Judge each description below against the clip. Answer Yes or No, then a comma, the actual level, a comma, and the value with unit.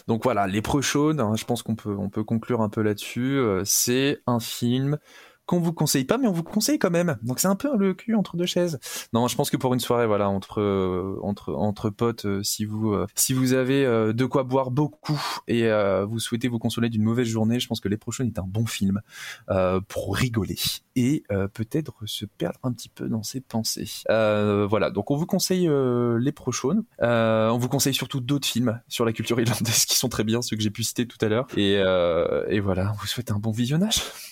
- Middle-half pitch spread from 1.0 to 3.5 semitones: No, average, 4.4 semitones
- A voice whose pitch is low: Yes, low, 120 Hz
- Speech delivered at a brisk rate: Yes, fast, 240 wpm